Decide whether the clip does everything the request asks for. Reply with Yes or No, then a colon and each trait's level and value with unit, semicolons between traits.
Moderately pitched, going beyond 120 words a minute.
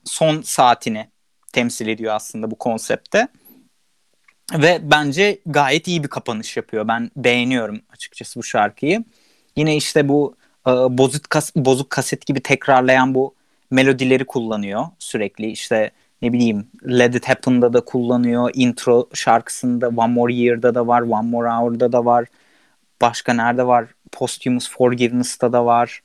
No: low, 125 Hz; fast, 140 wpm